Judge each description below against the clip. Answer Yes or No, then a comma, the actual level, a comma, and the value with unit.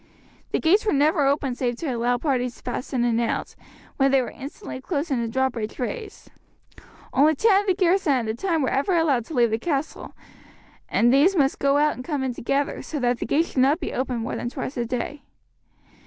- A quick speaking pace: Yes, fast, 225 wpm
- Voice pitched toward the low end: No, very high, 275 Hz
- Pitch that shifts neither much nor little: Yes, average, 4.2 semitones